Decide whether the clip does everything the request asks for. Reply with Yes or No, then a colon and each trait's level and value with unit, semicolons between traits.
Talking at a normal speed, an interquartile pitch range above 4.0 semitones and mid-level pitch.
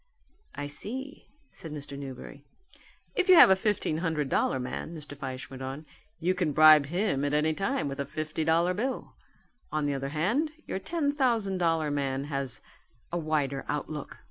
Yes: average, 175 wpm; average, 5.1 semitones; medium, 155 Hz